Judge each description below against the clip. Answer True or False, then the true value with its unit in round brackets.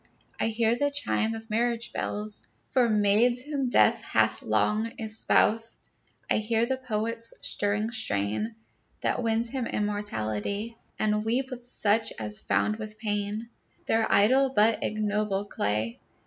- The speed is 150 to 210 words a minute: False (135 wpm)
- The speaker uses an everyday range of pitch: False (2.1 semitones)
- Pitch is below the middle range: False (220 Hz)